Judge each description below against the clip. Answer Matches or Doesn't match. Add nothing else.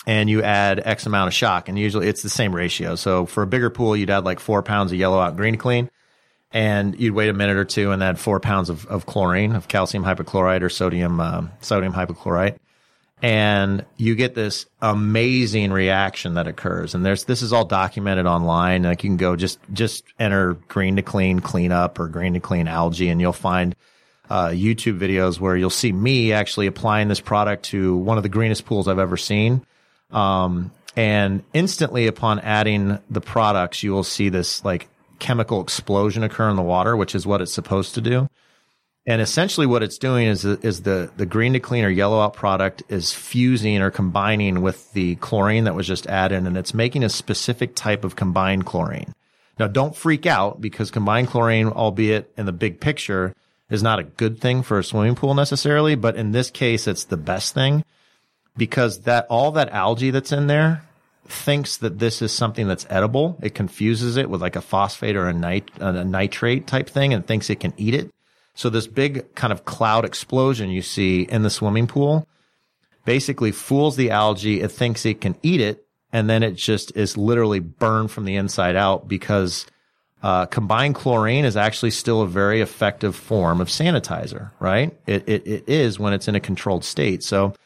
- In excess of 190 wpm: Matches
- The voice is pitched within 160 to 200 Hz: Doesn't match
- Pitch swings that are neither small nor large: Matches